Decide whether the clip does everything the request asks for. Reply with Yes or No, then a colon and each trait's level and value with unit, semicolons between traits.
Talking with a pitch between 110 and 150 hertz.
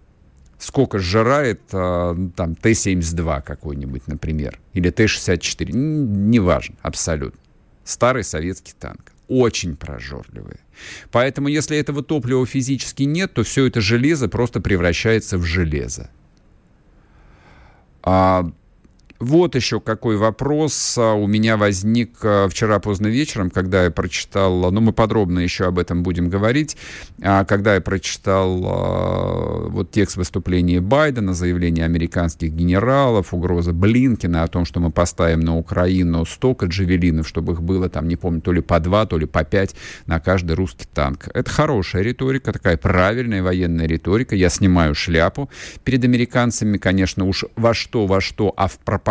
No: very low, 95 Hz